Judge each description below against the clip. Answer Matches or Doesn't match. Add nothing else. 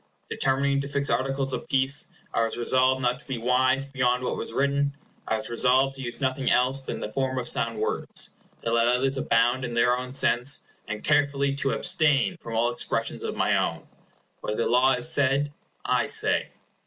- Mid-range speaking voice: Doesn't match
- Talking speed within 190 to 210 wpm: Matches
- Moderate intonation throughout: Doesn't match